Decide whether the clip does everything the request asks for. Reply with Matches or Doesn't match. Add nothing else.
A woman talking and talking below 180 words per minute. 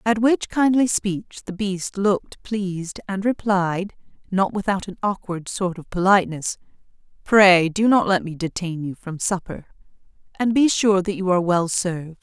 Matches